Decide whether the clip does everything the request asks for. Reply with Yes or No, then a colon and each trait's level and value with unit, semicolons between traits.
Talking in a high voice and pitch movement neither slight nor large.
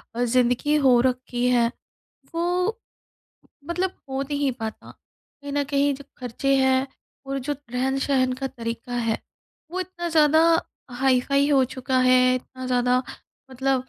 No: very high, 265 Hz; narrow, 2.3 semitones